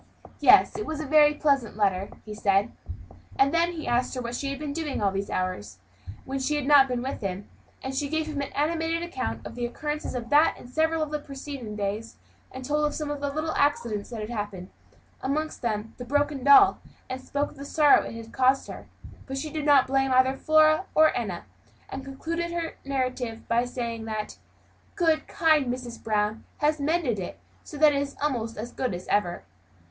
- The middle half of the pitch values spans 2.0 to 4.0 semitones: No, average, 4.7 semitones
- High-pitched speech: Yes, very high, 270 Hz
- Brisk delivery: Yes, fast, 210 wpm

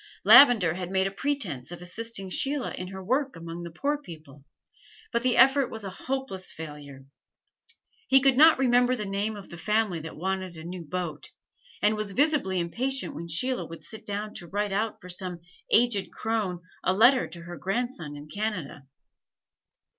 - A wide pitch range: Yes, wide, 5.9 semitones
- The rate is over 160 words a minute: Yes, average, 175 wpm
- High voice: Yes, high, 195 Hz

